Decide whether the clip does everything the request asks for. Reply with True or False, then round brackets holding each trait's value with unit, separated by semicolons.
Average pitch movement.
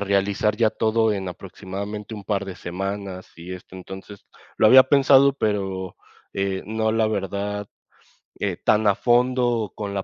False (2.2 semitones)